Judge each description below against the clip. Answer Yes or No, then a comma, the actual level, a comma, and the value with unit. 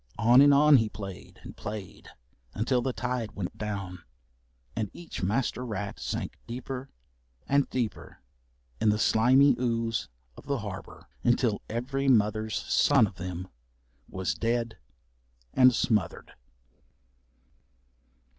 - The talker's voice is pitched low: Yes, low, 115 Hz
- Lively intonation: No, average, 3.4 semitones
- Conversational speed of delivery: No, slow, 120 wpm